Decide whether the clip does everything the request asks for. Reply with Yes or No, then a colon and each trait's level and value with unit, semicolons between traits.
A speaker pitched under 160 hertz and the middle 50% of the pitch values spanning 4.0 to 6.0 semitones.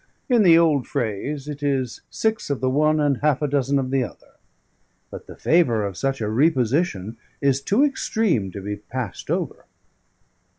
Yes: low, 135 Hz; average, 4.4 semitones